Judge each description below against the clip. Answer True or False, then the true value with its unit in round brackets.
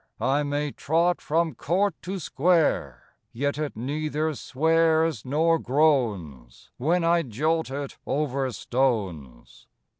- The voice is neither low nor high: True (145 Hz)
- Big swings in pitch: False (4.5 semitones)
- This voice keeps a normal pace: False (115 wpm)